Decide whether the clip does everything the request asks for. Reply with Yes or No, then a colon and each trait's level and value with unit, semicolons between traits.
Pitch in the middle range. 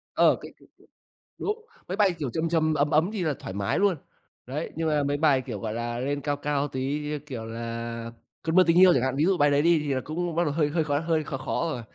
Yes: medium, 150 Hz